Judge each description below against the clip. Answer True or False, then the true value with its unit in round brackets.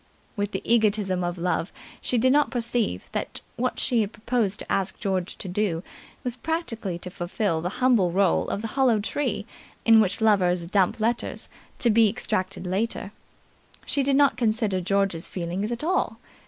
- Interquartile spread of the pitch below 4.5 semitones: True (4.1 semitones)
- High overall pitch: True (210 Hz)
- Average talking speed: True (165 wpm)